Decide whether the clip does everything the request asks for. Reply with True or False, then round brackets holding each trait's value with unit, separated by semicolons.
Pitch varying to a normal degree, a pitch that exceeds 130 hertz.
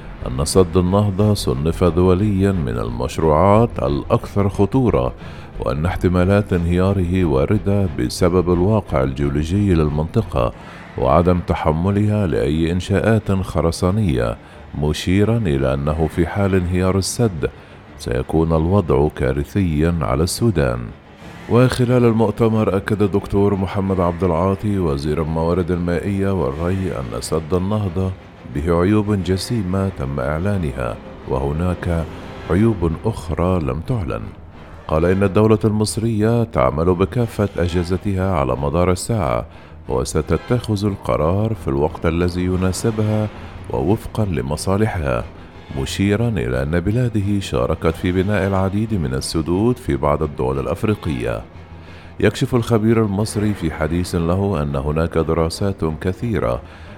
False (4.2 semitones; 90 Hz)